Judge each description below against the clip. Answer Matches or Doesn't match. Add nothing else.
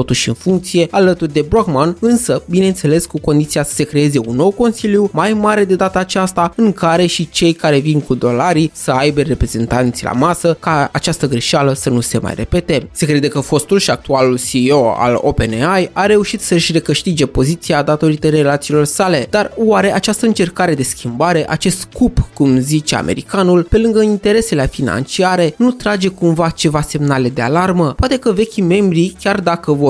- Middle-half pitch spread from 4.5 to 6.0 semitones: Matches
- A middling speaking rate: Doesn't match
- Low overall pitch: Doesn't match